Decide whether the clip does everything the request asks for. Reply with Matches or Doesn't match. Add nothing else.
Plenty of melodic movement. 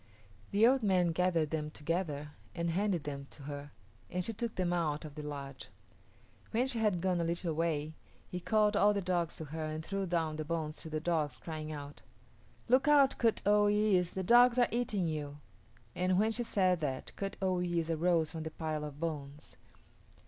Doesn't match